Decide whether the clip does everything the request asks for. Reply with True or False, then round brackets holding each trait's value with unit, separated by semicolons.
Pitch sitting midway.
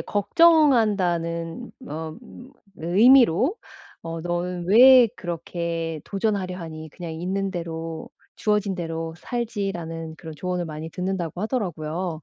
True (175 Hz)